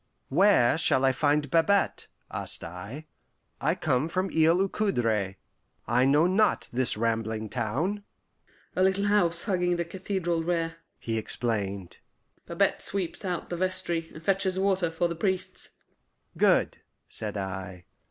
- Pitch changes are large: Yes, wide, 8.0 semitones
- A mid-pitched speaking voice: Yes, medium, 165 Hz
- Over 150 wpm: No, average, 140 wpm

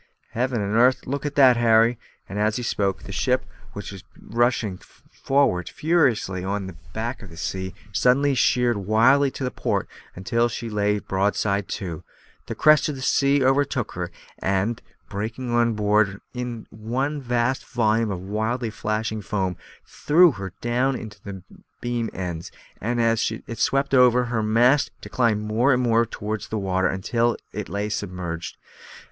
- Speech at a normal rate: Yes, average, 165 wpm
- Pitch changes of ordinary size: Yes, average, 3.7 semitones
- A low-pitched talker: Yes, low, 115 Hz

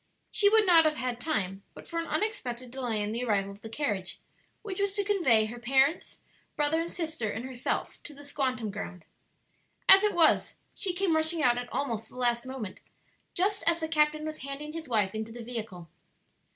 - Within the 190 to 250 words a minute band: Yes, average, 200 wpm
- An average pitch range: No, wide, 6.2 semitones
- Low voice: No, very high, 265 Hz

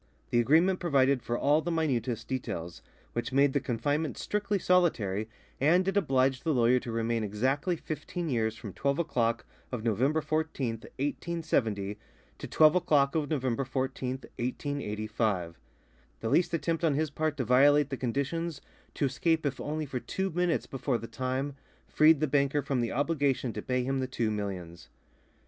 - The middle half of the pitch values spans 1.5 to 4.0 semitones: No, average, 4.7 semitones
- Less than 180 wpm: Yes, average, 165 wpm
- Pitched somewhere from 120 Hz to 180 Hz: Yes, low, 135 Hz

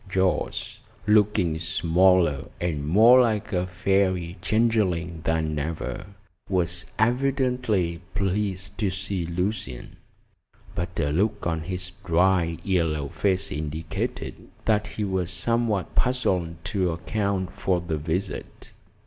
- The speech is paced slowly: Yes, slow, 115 wpm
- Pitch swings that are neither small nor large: Yes, average, 3.6 semitones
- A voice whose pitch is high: No, very low, 90 Hz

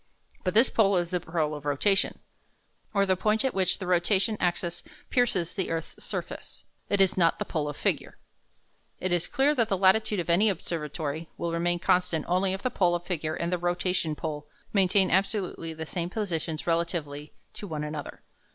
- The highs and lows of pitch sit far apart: No, average, 3.0 semitones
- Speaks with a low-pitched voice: No, medium, 175 Hz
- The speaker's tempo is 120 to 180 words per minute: No, average, 190 wpm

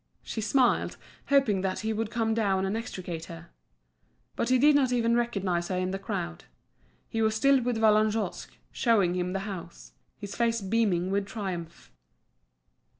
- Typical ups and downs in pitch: Yes, average, 3.7 semitones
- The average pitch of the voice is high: Yes, high, 210 Hz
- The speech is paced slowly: No, average, 160 wpm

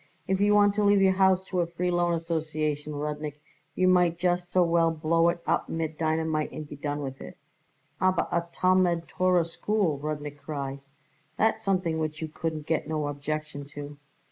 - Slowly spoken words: No, average, 185 wpm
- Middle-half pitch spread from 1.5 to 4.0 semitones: Yes, average, 3.0 semitones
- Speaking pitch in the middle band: Yes, medium, 165 Hz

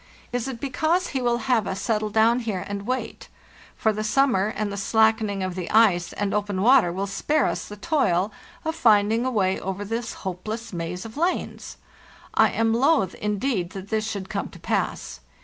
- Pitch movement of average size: Yes, average, 3.6 semitones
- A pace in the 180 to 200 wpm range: Yes, average, 190 wpm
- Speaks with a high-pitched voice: Yes, high, 215 Hz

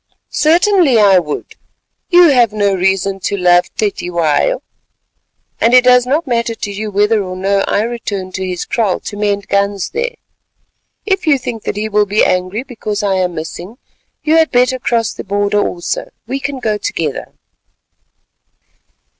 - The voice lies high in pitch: Yes, high, 210 Hz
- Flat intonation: No, average, 4.4 semitones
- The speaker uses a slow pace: No, average, 165 wpm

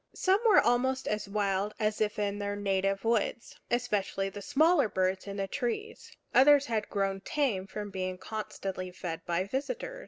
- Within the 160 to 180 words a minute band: Yes, average, 165 wpm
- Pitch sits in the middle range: No, high, 205 Hz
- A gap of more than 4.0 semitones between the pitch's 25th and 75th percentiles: Yes, average, 4.6 semitones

